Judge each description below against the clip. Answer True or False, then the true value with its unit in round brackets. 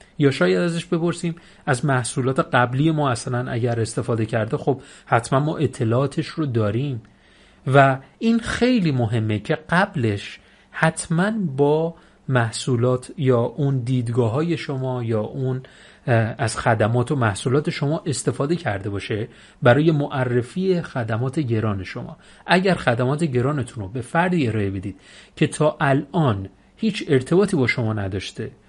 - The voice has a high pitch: False (130 Hz)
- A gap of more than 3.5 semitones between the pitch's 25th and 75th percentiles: True (5.1 semitones)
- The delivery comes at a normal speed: True (130 wpm)